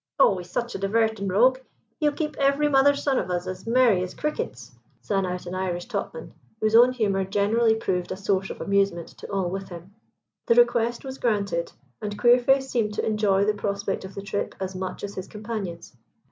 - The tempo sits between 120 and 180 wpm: No, average, 200 wpm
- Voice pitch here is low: No, high, 205 Hz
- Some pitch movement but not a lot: Yes, average, 4.1 semitones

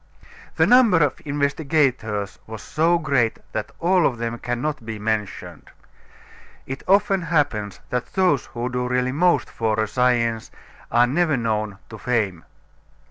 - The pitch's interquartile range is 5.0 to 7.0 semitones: Yes, wide, 5.5 semitones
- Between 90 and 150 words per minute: Yes, average, 140 wpm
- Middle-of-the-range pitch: No, low, 125 Hz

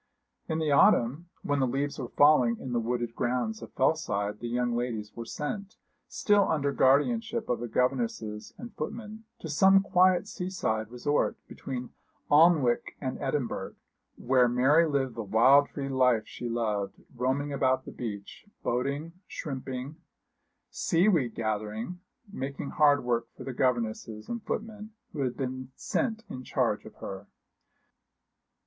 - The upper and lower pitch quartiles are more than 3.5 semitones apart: Yes, average, 5.1 semitones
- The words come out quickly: No, average, 140 wpm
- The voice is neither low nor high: No, low, 130 Hz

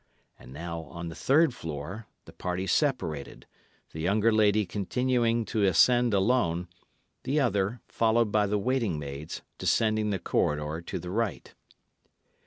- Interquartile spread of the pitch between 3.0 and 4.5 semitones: No, wide, 5.6 semitones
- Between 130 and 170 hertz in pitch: No, low, 105 Hz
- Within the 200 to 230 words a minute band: No, average, 140 wpm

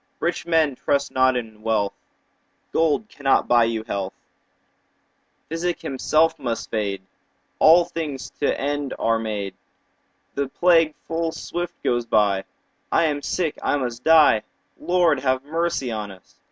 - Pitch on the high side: No, medium, 140 Hz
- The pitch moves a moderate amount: No, wide, 6.3 semitones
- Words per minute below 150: Yes, average, 140 wpm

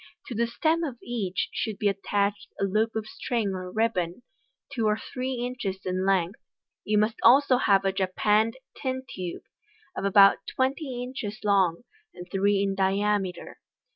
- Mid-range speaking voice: No, high, 210 Hz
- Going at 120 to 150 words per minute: No, average, 160 wpm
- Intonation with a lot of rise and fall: No, average, 3.8 semitones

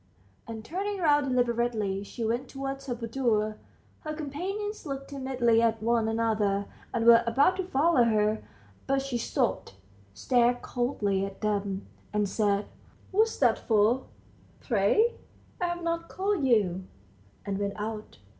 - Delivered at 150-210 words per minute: No, slow, 135 wpm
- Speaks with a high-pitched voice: Yes, high, 235 Hz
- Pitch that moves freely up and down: No, average, 4.7 semitones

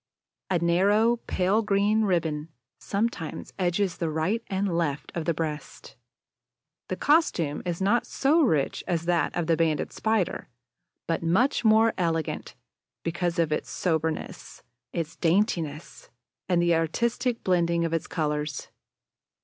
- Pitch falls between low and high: Yes, medium, 170 Hz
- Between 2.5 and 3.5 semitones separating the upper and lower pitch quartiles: No, average, 4.0 semitones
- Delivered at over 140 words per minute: No, slow, 135 wpm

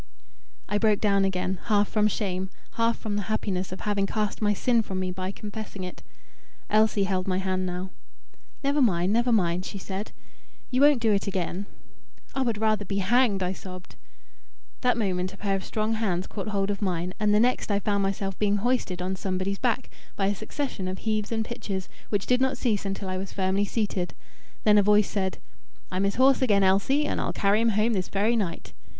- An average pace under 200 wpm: No, fast, 205 wpm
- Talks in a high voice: Yes, high, 200 Hz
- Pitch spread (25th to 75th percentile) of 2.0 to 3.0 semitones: Yes, narrow, 2.6 semitones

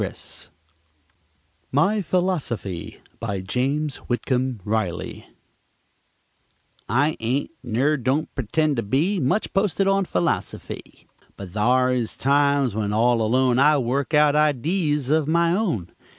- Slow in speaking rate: Yes, slow, 120 wpm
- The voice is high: No, low, 135 Hz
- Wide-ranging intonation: No, average, 4.8 semitones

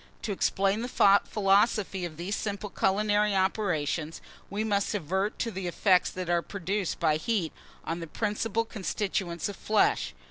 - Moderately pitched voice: No, high, 195 Hz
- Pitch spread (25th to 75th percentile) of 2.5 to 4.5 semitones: Yes, average, 3.1 semitones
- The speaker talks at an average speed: Yes, average, 150 wpm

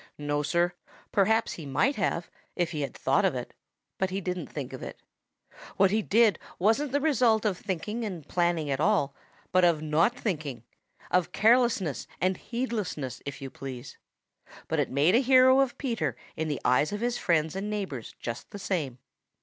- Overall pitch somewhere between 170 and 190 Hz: Yes, medium, 185 Hz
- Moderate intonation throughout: No, wide, 6.6 semitones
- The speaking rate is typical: Yes, average, 180 wpm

